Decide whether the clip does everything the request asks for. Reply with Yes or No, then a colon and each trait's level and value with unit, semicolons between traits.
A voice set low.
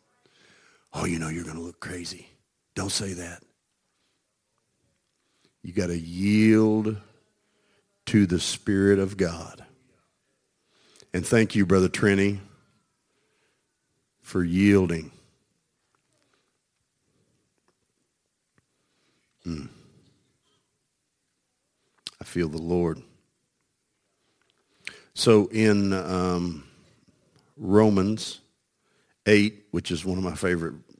Yes: very low, 95 Hz